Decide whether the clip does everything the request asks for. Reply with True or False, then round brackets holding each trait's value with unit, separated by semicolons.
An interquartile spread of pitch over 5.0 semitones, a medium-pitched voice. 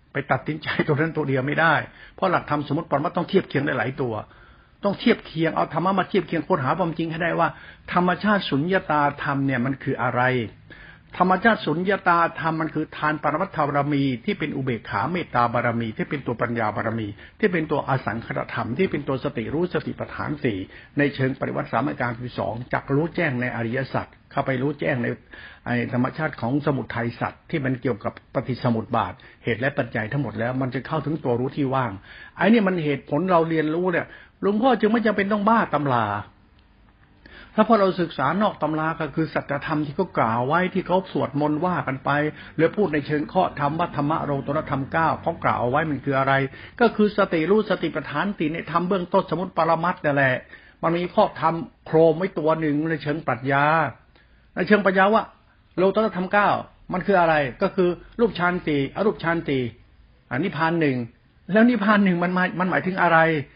True (5.4 semitones; 150 Hz)